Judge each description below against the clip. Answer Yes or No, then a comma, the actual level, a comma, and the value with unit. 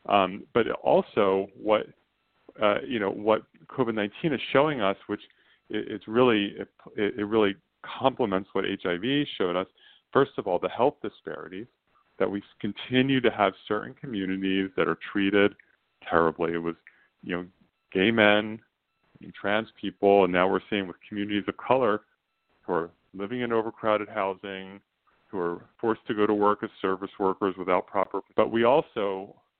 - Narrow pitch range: Yes, narrow, 2.3 semitones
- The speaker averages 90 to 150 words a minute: No, average, 165 wpm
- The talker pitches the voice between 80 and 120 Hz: Yes, low, 100 Hz